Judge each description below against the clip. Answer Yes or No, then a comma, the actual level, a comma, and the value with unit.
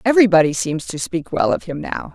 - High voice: No, medium, 175 Hz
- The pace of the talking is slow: No, fast, 225 wpm